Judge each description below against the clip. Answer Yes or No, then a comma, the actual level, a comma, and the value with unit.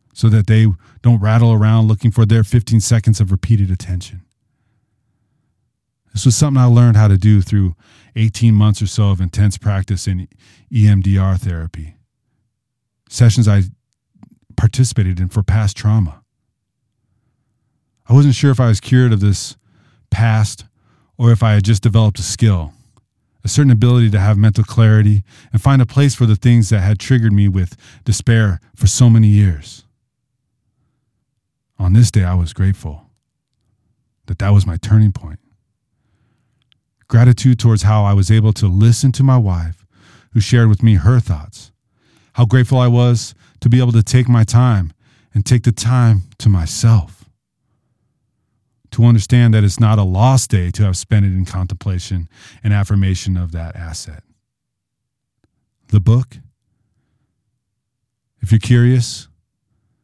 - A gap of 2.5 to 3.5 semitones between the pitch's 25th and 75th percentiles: Yes, average, 2.9 semitones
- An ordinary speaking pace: Yes, average, 150 wpm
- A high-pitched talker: No, low, 110 Hz